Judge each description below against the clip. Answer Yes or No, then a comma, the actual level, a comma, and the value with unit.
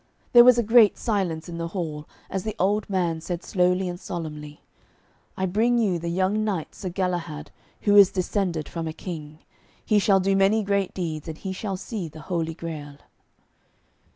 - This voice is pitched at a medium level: Yes, medium, 180 Hz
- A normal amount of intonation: Yes, average, 3.5 semitones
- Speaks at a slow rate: No, average, 180 wpm